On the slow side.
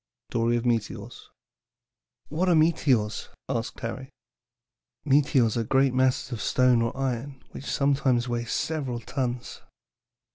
Yes: slow, 130 wpm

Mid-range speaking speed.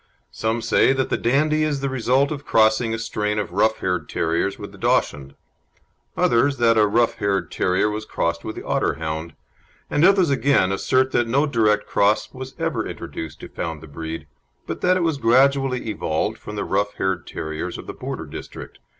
Yes: average, 190 wpm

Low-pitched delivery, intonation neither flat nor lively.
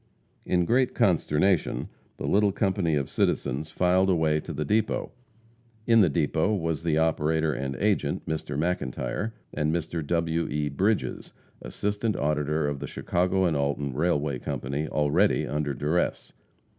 Yes: very low, 80 Hz; average, 3.9 semitones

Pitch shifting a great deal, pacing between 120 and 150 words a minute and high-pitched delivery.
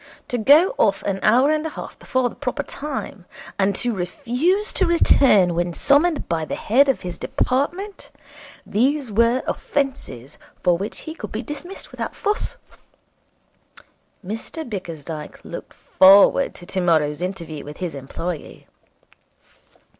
Yes: wide, 8.3 semitones; average, 140 wpm; high, 225 Hz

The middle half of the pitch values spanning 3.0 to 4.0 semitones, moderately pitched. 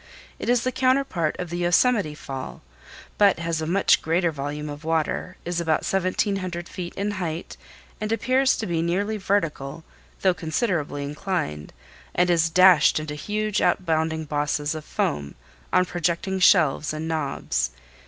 Yes: average, 3.7 semitones; medium, 170 Hz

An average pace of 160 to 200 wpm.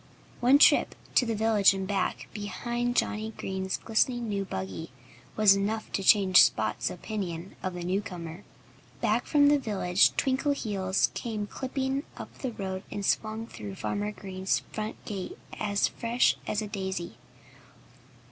No: average, 145 wpm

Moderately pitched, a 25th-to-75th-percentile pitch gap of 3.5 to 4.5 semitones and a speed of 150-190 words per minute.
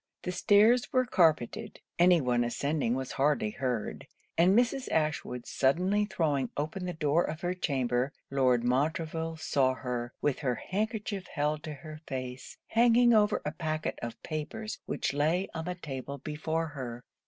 No: medium, 155 Hz; average, 5.3 semitones; average, 155 wpm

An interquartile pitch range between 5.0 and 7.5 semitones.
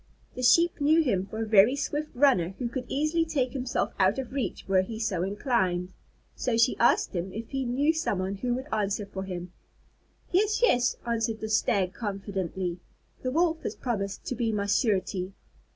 Yes: wide, 5.4 semitones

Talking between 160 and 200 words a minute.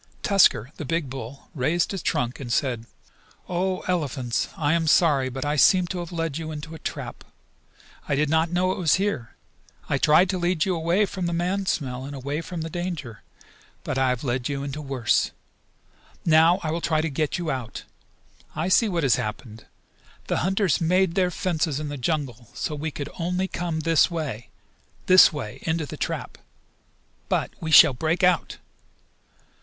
Yes: average, 185 wpm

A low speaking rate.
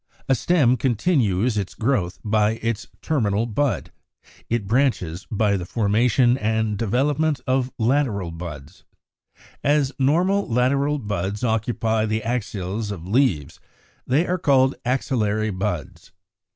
Yes: slow, 120 wpm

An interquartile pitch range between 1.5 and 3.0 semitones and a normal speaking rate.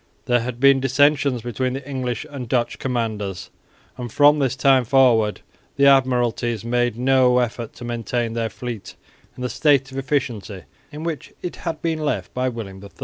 Yes: narrow, 2.6 semitones; average, 175 wpm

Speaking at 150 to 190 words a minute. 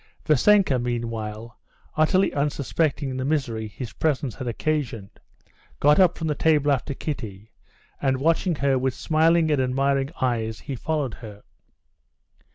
No: slow, 135 wpm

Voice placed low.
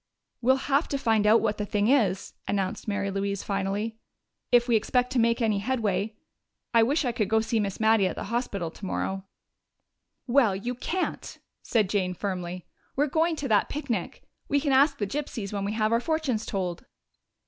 No: high, 220 Hz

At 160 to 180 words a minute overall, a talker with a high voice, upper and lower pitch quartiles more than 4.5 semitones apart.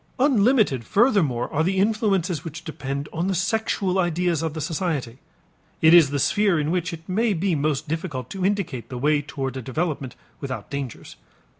No: average, 175 wpm; medium, 165 Hz; average, 5.2 semitones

